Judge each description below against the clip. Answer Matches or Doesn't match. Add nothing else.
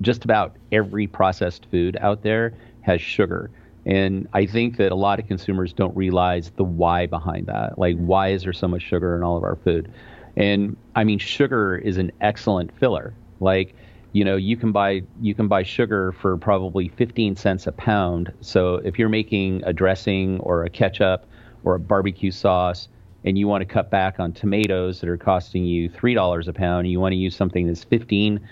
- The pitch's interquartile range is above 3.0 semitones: Doesn't match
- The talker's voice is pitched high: Doesn't match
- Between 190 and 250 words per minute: Matches